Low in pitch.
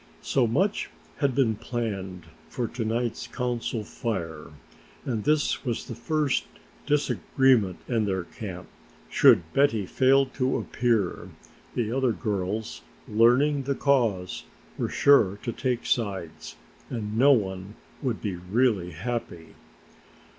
Yes: low, 115 Hz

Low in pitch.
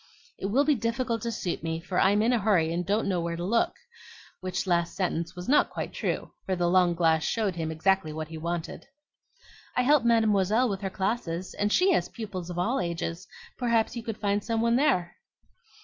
No: high, 195 Hz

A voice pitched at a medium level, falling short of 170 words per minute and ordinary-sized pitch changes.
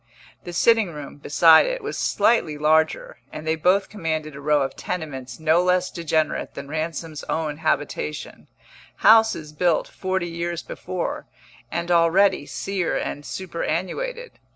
Yes: medium, 165 Hz; slow, 135 wpm; average, 3.0 semitones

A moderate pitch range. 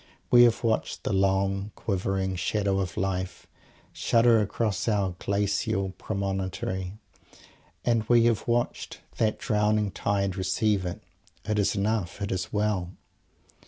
No: narrow, 2.1 semitones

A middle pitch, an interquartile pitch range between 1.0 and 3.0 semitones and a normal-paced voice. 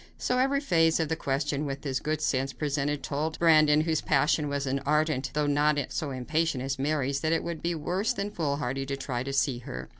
No: medium, 150 Hz; narrow, 2.6 semitones; fast, 215 wpm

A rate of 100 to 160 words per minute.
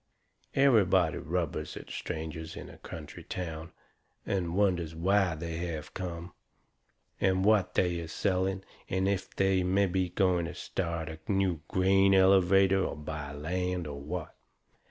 Yes: average, 145 wpm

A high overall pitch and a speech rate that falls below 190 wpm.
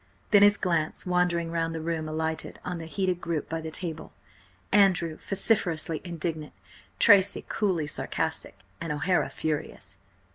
No: medium, 165 Hz; average, 140 wpm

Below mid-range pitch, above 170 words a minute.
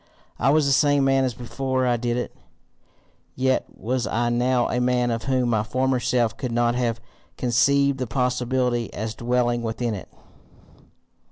No: low, 125 Hz; average, 165 wpm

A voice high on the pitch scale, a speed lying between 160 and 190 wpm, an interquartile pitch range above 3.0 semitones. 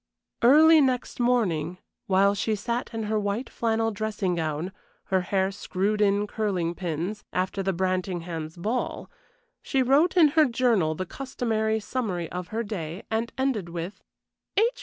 No: high, 205 Hz; average, 150 wpm; average, 4.4 semitones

